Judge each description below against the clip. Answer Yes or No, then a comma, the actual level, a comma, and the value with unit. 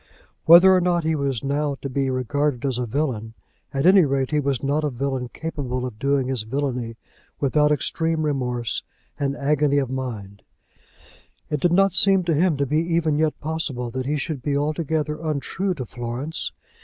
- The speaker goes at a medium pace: Yes, average, 180 wpm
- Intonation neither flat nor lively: Yes, average, 3.4 semitones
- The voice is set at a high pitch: No, medium, 140 Hz